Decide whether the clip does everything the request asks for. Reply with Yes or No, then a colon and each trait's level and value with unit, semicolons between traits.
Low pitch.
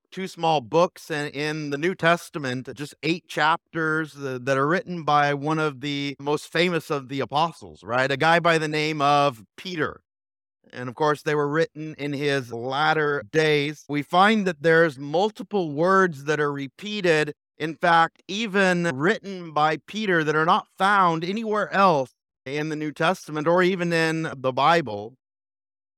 No: medium, 155 Hz